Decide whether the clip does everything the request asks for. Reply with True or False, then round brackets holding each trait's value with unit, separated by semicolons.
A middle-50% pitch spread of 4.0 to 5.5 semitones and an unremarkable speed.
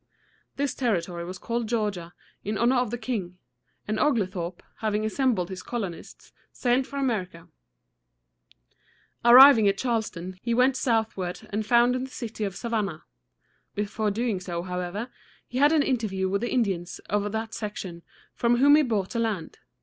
True (4.4 semitones; 155 wpm)